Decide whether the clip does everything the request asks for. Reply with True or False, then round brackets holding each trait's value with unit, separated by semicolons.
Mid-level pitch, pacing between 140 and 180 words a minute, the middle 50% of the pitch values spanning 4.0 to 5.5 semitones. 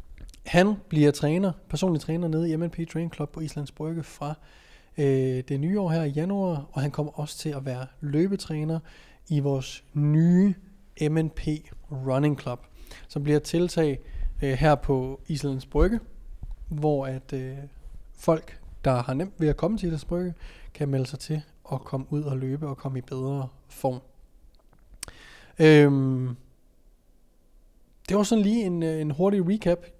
False (150 Hz; 160 wpm; 3.6 semitones)